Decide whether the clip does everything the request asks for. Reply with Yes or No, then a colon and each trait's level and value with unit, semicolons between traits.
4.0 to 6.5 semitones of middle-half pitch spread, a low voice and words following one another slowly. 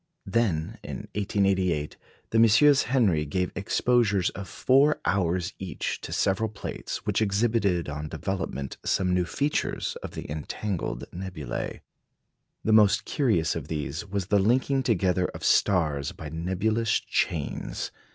Yes: average, 4.5 semitones; very low, 95 Hz; slow, 130 wpm